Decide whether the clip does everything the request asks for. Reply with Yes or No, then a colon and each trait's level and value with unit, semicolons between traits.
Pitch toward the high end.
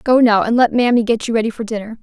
Yes: high, 230 Hz